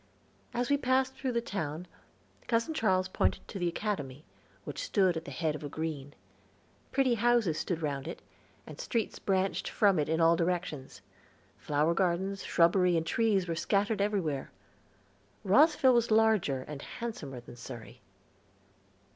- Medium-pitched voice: Yes, medium, 180 Hz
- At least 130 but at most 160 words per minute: Yes, average, 150 wpm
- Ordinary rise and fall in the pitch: No, wide, 6.4 semitones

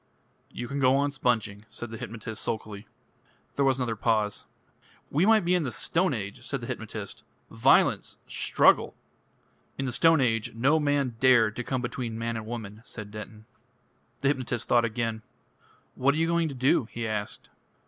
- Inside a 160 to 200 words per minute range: Yes, average, 175 wpm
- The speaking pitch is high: No, low, 120 Hz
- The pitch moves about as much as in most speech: Yes, average, 3.8 semitones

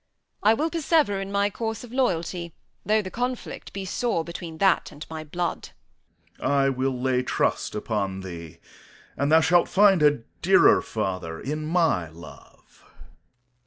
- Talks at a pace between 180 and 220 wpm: No, average, 155 wpm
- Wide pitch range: Yes, wide, 7.5 semitones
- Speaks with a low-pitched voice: No, medium, 165 Hz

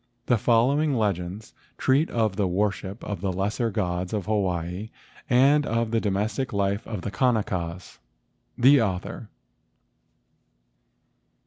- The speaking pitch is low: Yes, low, 105 Hz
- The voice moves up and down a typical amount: Yes, average, 3.7 semitones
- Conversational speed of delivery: No, slow, 125 wpm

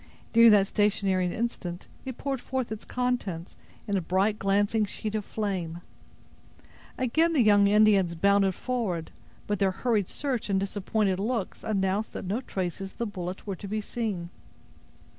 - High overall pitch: Yes, high, 205 Hz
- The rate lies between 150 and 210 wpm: Yes, average, 160 wpm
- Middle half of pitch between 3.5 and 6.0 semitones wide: No, average, 2.8 semitones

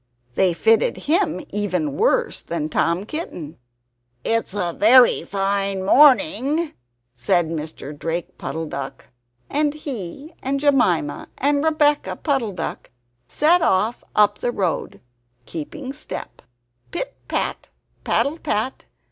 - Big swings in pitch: Yes, wide, 8.9 semitones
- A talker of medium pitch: No, high, 210 Hz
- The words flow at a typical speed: No, slow, 115 wpm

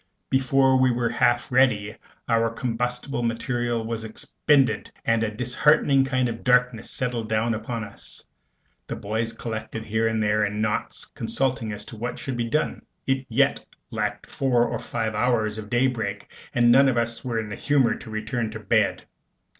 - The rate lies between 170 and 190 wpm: Yes, average, 175 wpm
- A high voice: No, low, 115 Hz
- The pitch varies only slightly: Yes, narrow, 2.3 semitones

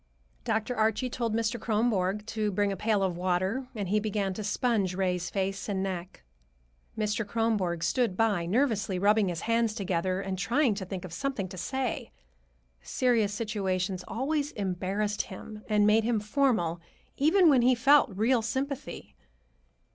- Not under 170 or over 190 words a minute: No, average, 155 wpm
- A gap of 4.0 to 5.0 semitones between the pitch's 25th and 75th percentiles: No, average, 3.6 semitones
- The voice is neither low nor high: No, high, 210 Hz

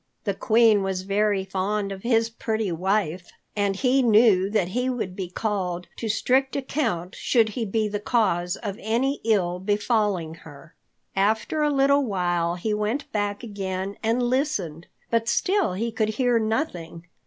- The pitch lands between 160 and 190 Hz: No, high, 210 Hz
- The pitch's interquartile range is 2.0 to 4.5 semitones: Yes, average, 3.7 semitones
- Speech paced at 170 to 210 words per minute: No, average, 160 wpm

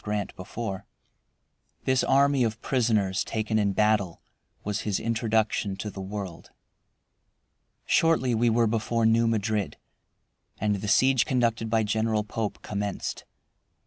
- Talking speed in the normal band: No, slow, 125 wpm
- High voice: No, low, 110 Hz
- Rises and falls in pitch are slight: Yes, narrow, 2.1 semitones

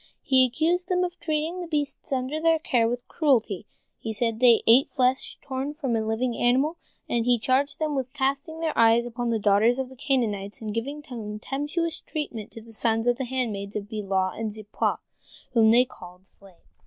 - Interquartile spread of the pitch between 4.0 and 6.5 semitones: Yes, average, 4.4 semitones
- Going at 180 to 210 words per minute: Yes, average, 185 wpm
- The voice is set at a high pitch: Yes, high, 245 Hz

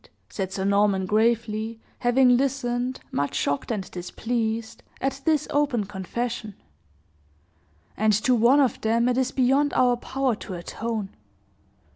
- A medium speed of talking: No, slow, 130 wpm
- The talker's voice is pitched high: Yes, high, 235 Hz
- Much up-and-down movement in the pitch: No, average, 3.4 semitones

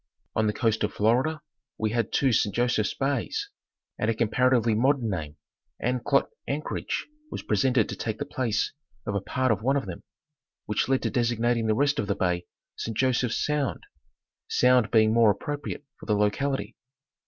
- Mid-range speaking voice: No, low, 115 Hz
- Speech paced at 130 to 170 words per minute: No, average, 185 wpm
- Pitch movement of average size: Yes, average, 3.5 semitones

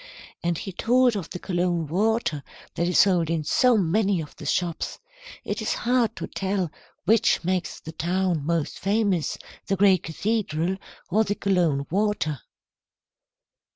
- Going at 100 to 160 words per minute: Yes, average, 150 wpm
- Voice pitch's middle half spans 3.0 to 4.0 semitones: Yes, average, 3.7 semitones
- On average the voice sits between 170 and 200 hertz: Yes, medium, 185 Hz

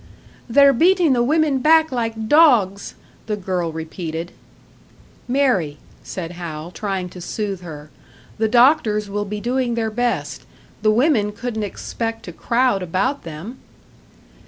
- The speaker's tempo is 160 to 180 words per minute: No, slow, 135 wpm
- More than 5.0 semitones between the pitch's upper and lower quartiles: Yes, wide, 5.6 semitones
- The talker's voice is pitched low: No, high, 220 Hz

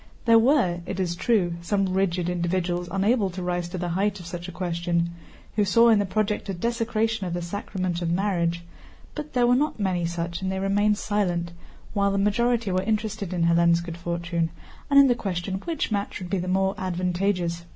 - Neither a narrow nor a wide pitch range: Yes, average, 3.3 semitones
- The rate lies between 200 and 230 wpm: Yes, fast, 205 wpm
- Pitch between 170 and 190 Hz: Yes, medium, 185 Hz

